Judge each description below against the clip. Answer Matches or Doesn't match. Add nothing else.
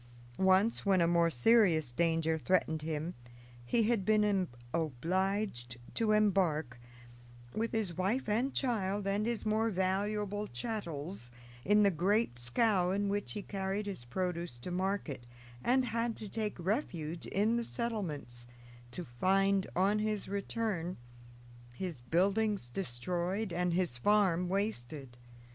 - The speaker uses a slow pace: Matches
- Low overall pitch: Doesn't match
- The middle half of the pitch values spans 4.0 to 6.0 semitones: Matches